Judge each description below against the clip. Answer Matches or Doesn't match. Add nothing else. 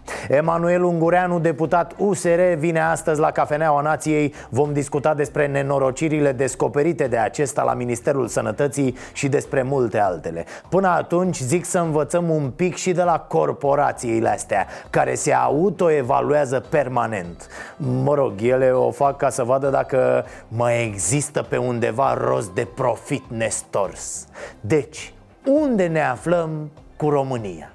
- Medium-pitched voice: Matches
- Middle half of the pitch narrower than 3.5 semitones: Doesn't match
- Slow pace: Doesn't match